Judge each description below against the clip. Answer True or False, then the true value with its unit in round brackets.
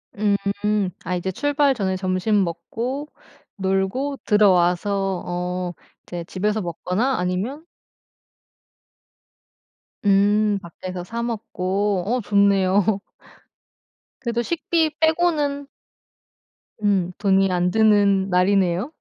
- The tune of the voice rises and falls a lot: False (3.8 semitones)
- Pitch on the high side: True (200 Hz)